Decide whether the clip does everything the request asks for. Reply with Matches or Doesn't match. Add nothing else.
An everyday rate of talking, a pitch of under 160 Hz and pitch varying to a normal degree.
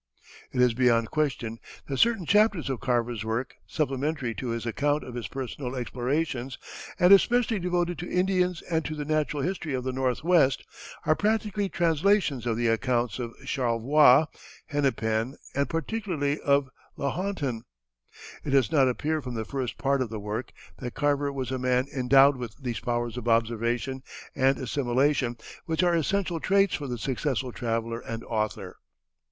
Matches